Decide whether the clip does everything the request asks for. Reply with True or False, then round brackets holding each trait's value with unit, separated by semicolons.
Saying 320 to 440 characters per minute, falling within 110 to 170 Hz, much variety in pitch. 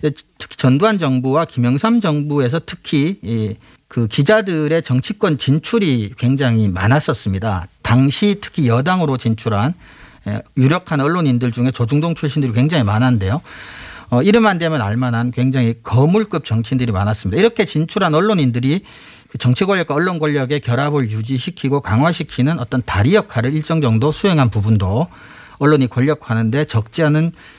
False (350 characters per minute; 135 Hz; 4.8 semitones)